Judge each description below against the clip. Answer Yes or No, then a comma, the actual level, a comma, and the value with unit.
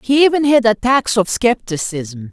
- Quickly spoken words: No, average, 155 wpm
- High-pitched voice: Yes, high, 225 Hz